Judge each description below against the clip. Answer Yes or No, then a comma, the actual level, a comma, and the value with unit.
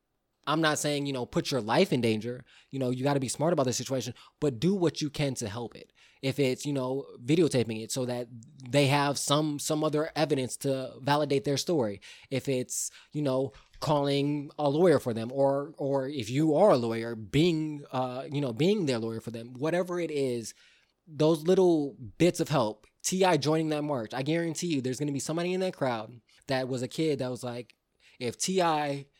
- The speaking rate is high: Yes, fast, 210 wpm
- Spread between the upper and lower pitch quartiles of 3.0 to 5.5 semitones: Yes, average, 3.5 semitones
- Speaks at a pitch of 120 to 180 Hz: Yes, medium, 140 Hz